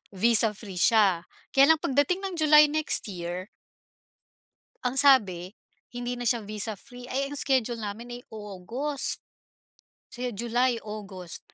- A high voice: Yes, high, 235 Hz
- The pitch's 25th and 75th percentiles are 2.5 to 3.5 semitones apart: No, average, 4.6 semitones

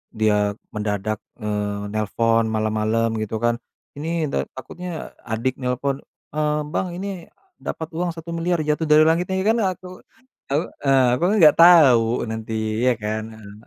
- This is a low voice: Yes, low, 130 Hz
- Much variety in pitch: Yes, wide, 7.3 semitones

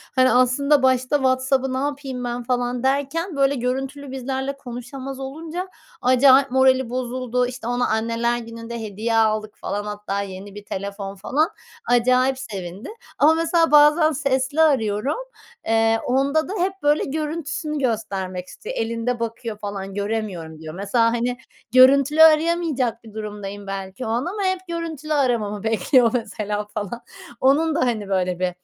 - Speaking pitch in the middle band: No, very high, 250 Hz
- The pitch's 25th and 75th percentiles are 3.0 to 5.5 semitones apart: Yes, average, 4.4 semitones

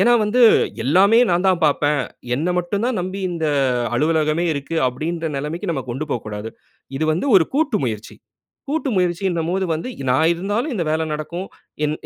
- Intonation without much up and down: No, average, 4.1 semitones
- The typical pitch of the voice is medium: Yes, medium, 170 Hz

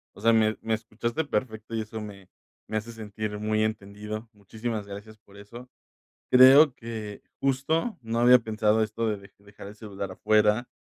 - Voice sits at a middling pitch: No, low, 110 Hz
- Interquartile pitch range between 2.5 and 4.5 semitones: No, narrow, 1.8 semitones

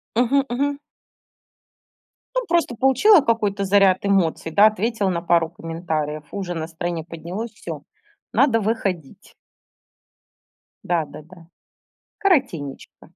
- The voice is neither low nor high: No, high, 195 Hz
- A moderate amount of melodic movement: No, wide, 5.8 semitones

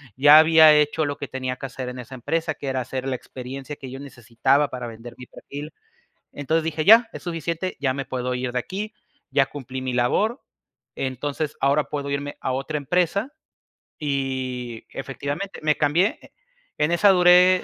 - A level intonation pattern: No, average, 3.6 semitones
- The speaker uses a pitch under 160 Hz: Yes, medium, 140 Hz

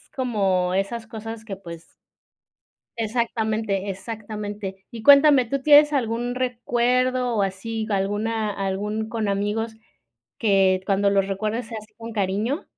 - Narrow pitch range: No, average, 3.0 semitones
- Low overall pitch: No, high, 220 Hz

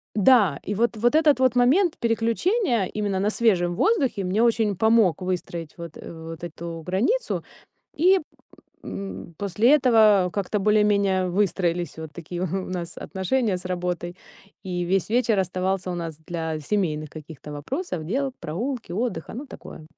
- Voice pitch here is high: Yes, high, 195 Hz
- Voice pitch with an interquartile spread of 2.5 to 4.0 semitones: No, average, 5.0 semitones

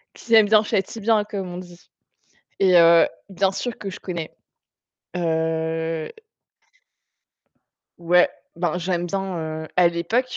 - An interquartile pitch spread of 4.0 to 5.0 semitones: No, average, 2.9 semitones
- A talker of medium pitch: Yes, medium, 180 Hz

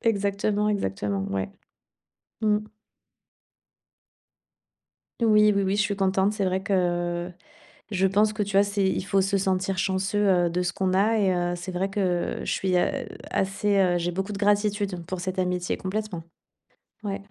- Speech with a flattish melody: Yes, narrow, 2.2 semitones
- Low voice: No, high, 195 Hz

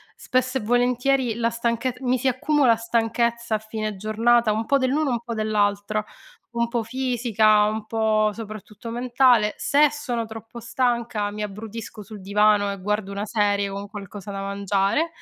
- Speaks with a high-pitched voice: Yes, high, 225 Hz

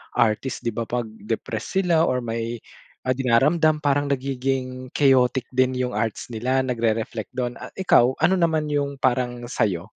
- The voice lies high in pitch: No, low, 125 Hz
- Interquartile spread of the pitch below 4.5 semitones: Yes, average, 2.8 semitones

